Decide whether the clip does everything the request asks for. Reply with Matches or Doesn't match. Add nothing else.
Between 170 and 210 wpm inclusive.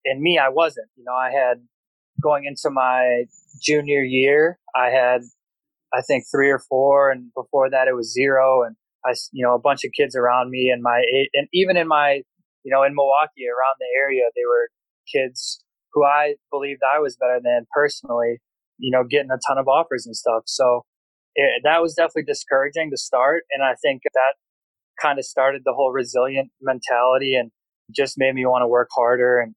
Matches